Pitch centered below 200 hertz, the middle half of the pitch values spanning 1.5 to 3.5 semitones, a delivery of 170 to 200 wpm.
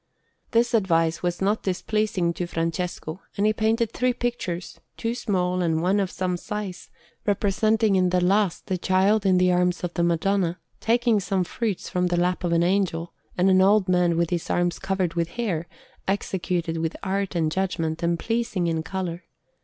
Yes: medium, 185 Hz; average, 2.9 semitones; average, 180 wpm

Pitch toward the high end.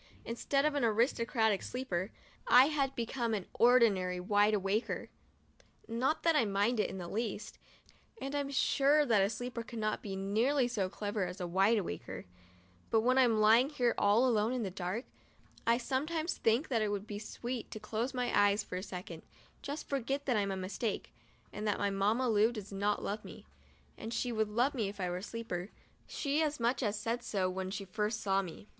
Yes: high, 220 Hz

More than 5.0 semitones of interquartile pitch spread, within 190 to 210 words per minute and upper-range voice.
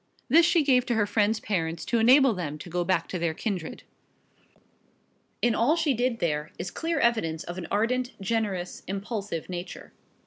No: wide, 5.6 semitones; average, 175 wpm; high, 205 Hz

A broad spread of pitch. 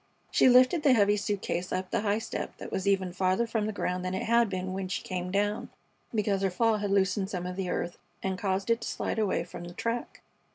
No: average, 2.8 semitones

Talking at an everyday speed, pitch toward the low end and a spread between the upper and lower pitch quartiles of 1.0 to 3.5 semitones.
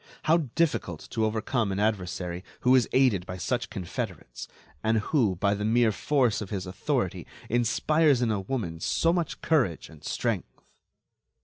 No: average, 155 wpm; low, 110 Hz; average, 5.1 semitones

